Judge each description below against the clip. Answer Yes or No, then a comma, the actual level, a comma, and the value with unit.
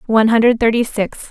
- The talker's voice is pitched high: Yes, high, 225 Hz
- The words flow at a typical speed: Yes, average, 185 wpm